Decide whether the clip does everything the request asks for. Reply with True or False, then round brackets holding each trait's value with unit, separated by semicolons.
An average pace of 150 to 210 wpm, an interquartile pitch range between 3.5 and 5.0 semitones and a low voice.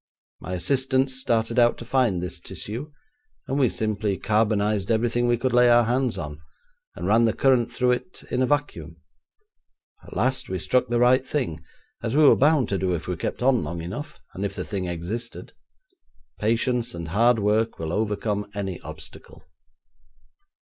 True (175 wpm; 4.4 semitones; 115 Hz)